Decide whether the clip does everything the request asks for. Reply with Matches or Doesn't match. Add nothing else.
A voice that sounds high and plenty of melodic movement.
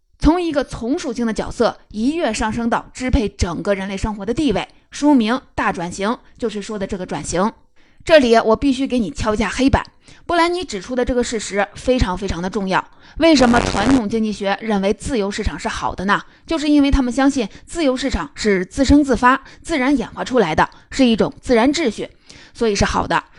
Doesn't match